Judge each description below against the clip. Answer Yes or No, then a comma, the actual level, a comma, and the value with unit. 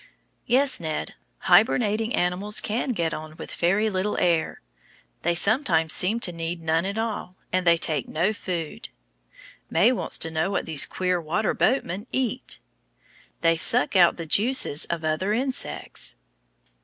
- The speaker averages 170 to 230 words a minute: No, average, 150 wpm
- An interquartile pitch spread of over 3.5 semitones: Yes, average, 4.7 semitones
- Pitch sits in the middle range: Yes, medium, 180 Hz